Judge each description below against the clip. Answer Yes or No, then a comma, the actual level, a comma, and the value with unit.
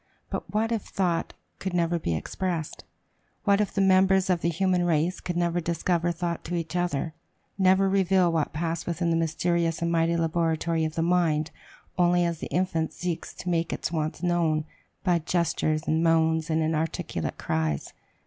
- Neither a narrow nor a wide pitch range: No, narrow, 1.7 semitones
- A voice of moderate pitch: Yes, medium, 170 Hz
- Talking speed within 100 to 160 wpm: No, average, 175 wpm